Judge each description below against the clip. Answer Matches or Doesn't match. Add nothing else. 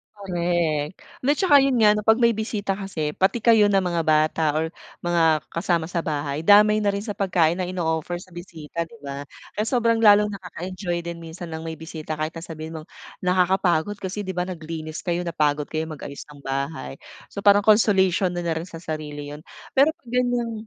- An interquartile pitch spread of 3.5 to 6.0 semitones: Matches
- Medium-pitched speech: Matches